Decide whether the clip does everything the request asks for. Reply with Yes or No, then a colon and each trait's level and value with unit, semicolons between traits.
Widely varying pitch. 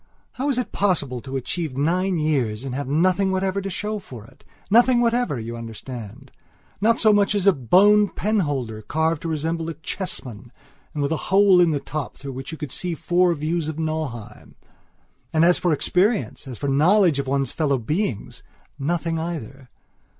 Yes: wide, 5.7 semitones